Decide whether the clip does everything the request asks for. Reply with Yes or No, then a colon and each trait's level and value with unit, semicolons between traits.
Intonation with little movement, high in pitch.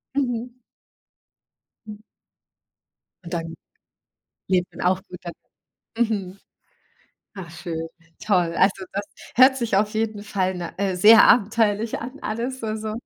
No: average, 3.7 semitones; high, 205 Hz